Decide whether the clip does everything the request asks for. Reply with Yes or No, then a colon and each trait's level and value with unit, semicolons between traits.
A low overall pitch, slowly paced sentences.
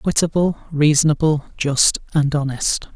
No: medium, 150 Hz; slow, 100 wpm